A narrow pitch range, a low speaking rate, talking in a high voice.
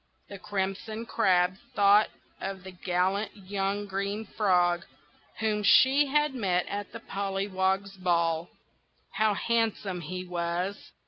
Yes: narrow, 2.2 semitones; slow, 120 wpm; high, 195 Hz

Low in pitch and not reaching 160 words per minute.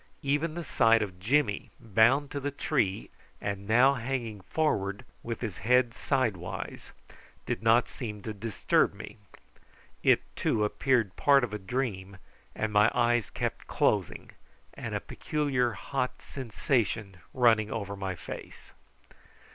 Yes: low, 115 Hz; slow, 135 wpm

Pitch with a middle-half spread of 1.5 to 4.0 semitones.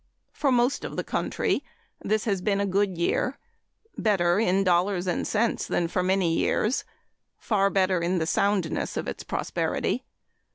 Yes: average, 2.8 semitones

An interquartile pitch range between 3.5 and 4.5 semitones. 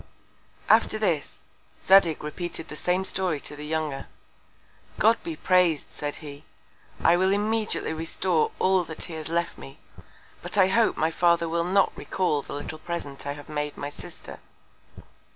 Yes: average, 3.8 semitones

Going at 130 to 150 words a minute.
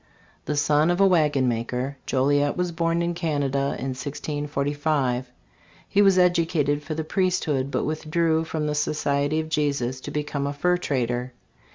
No: average, 160 wpm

